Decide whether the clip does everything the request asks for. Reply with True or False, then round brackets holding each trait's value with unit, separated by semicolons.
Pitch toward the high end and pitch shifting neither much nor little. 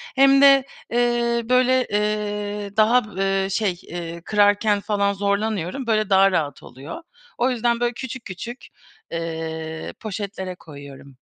True (205 Hz; 4.5 semitones)